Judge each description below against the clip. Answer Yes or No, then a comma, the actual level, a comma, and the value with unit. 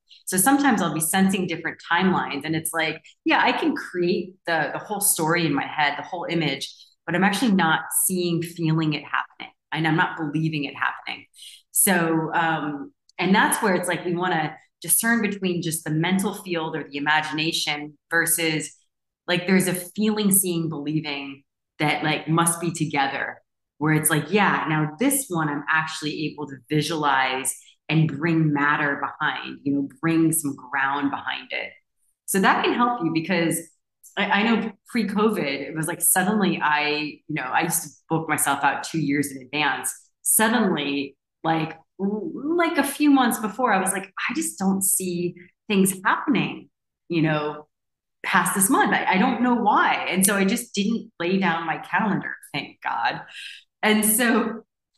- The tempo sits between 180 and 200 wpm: No, average, 170 wpm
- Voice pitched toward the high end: No, medium, 165 Hz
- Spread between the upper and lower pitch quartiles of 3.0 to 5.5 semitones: Yes, average, 4.5 semitones